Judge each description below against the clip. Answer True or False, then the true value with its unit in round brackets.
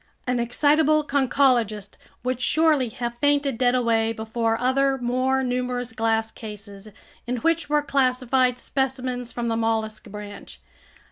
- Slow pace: True (130 wpm)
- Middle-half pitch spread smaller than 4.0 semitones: True (2.9 semitones)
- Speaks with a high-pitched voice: True (250 Hz)